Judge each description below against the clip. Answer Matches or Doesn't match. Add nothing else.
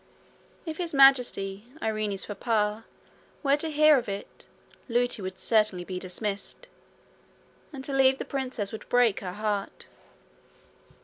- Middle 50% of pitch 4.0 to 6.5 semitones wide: Matches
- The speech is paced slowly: Matches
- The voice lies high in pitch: Matches